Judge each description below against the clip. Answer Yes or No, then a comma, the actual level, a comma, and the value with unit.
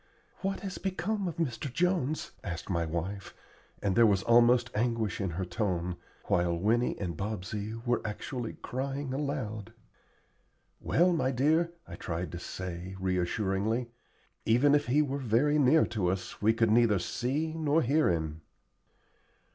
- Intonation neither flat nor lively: No, wide, 7.0 semitones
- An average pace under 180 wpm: Yes, average, 145 wpm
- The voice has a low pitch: Yes, low, 115 Hz